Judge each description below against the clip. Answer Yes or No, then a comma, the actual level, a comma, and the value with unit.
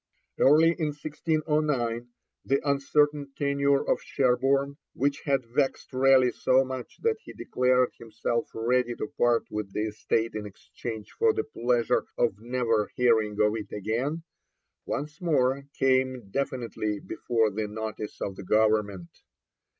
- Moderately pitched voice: No, low, 125 Hz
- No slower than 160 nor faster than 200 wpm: No, slow, 135 wpm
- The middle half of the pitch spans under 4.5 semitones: Yes, average, 4.1 semitones